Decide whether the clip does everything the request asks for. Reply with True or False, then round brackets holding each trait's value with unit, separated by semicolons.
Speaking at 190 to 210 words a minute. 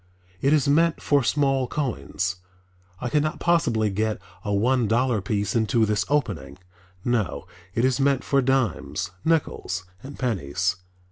False (145 wpm)